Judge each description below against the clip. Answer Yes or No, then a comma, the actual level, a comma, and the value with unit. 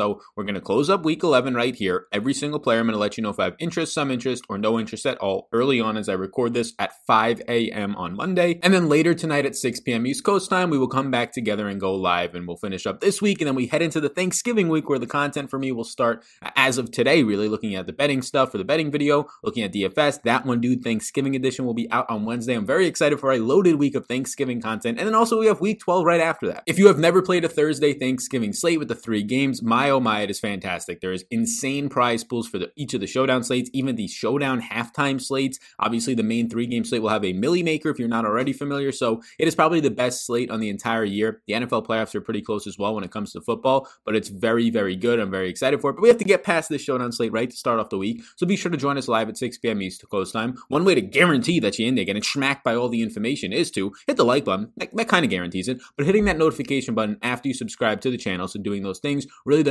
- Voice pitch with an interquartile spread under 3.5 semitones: No, average, 4.8 semitones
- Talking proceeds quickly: Yes, fast, 280 wpm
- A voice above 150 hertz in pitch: No, low, 125 Hz